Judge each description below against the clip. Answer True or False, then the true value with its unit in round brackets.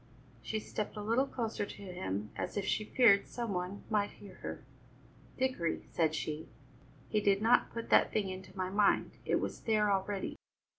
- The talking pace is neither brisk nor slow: True (180 wpm)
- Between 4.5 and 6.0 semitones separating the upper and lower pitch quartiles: False (2.7 semitones)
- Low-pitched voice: False (205 Hz)